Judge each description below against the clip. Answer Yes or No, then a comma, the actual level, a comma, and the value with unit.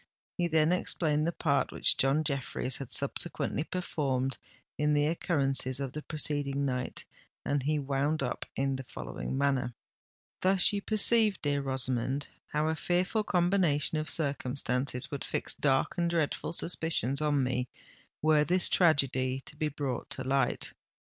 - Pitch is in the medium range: Yes, medium, 145 Hz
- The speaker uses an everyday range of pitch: Yes, average, 3.1 semitones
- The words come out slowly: No, average, 150 wpm